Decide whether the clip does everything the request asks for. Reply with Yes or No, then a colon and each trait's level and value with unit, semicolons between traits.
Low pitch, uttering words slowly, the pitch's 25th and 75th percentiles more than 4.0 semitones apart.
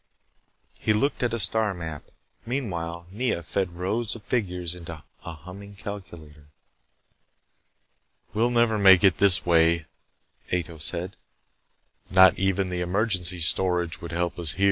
No: very low, 90 Hz; slow, 130 wpm; average, 3.2 semitones